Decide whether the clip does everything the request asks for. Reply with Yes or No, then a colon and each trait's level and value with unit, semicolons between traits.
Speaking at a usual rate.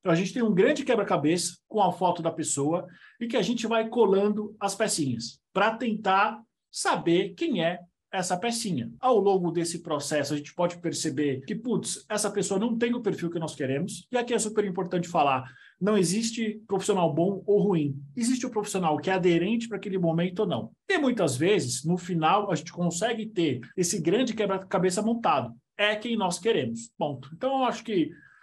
No: fast, 190 wpm